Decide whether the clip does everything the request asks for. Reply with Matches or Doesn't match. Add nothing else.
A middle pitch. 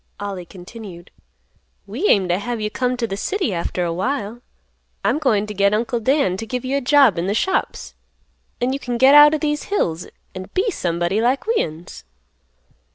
Doesn't match